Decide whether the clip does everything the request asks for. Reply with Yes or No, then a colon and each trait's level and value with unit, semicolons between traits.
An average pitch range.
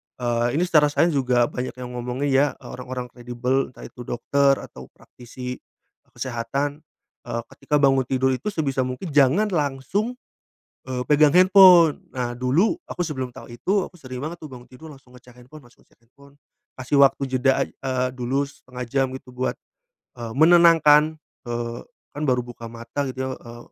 Yes: average, 3.0 semitones